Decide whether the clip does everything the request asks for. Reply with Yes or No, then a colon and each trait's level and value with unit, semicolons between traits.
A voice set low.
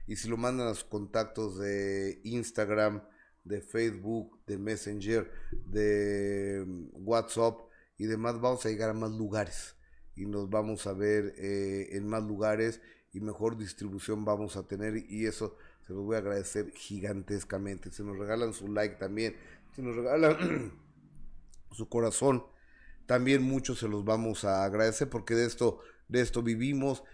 Yes: low, 110 Hz